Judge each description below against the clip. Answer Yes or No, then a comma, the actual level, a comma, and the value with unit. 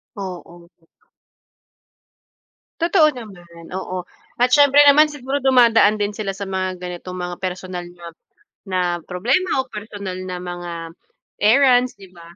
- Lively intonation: Yes, wide, 5.9 semitones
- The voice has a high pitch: Yes, high, 195 Hz